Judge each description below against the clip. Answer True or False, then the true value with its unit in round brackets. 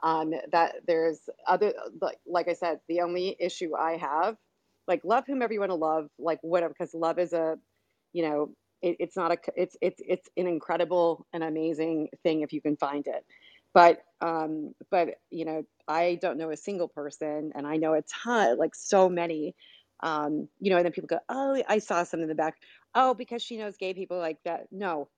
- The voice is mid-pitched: True (170 Hz)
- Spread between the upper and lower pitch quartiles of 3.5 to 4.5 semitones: False (2.8 semitones)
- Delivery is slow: False (205 wpm)